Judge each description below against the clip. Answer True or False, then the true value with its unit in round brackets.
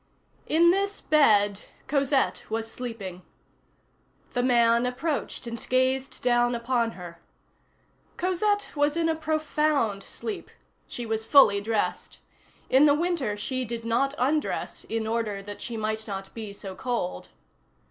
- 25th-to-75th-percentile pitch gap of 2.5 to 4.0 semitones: False (5.0 semitones)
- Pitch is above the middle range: True (240 Hz)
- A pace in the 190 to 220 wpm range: False (135 wpm)